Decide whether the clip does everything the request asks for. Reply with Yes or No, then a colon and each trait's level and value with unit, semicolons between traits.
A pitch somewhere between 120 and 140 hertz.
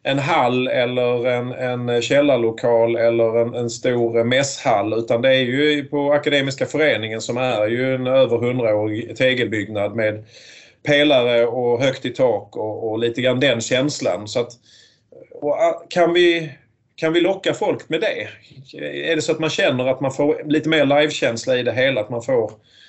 Yes: low, 130 Hz